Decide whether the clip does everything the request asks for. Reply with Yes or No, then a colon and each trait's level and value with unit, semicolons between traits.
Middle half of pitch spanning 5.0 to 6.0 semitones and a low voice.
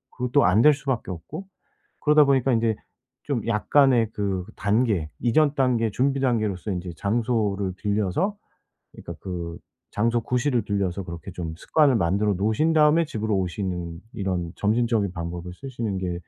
Yes: wide, 5.4 semitones; low, 110 Hz